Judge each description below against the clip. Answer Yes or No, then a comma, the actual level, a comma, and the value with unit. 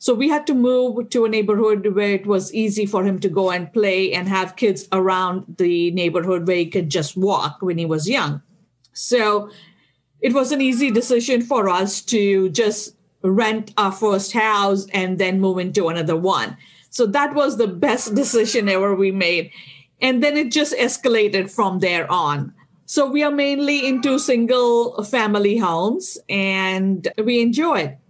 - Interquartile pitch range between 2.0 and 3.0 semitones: No, average, 4.6 semitones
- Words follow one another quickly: No, average, 175 wpm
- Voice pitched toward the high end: Yes, high, 205 Hz